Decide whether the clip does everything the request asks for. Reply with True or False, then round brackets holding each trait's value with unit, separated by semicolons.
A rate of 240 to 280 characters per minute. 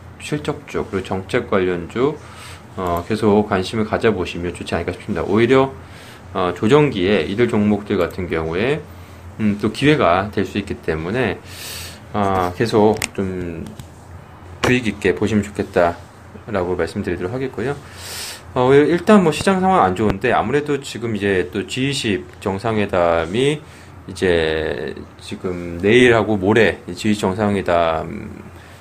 True (270 characters per minute)